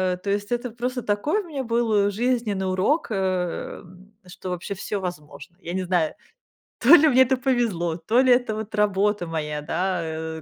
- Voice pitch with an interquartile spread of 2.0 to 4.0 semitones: No, average, 5.3 semitones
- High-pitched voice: Yes, high, 200 Hz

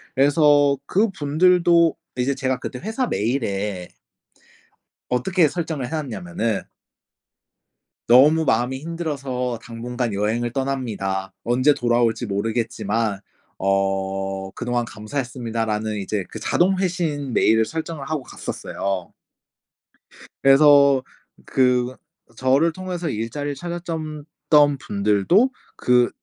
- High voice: No, low, 130 Hz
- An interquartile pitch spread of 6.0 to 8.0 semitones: No, wide, 5.5 semitones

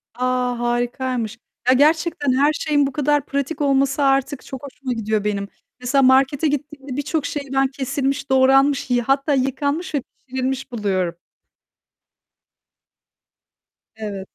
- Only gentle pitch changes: Yes, narrow, 2.3 semitones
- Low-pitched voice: No, very high, 270 Hz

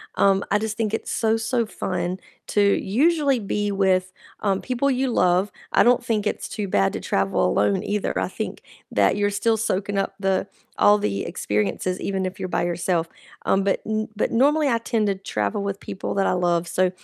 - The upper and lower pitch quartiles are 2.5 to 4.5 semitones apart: Yes, average, 3.3 semitones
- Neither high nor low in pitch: No, high, 200 Hz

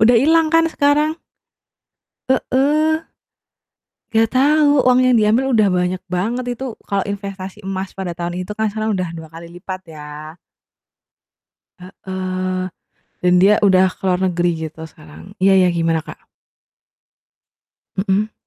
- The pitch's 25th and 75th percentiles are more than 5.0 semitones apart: Yes, wide, 5.4 semitones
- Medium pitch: No, high, 195 Hz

